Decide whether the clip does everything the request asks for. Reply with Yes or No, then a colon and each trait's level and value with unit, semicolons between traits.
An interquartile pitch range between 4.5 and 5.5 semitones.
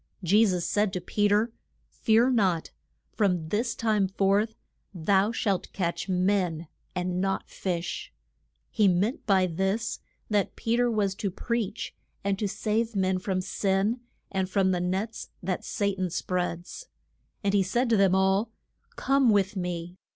No: average, 2.8 semitones